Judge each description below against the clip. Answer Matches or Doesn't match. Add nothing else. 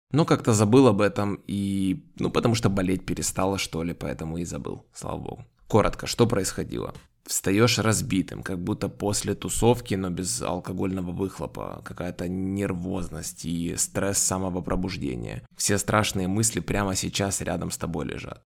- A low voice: Matches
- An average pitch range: Doesn't match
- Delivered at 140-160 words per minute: Matches